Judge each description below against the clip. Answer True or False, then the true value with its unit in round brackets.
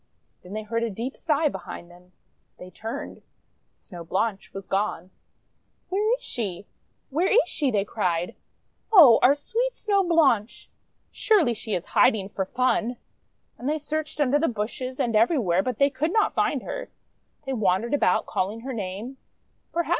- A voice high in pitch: True (235 Hz)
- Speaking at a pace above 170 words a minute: False (165 wpm)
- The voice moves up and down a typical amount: False (7.2 semitones)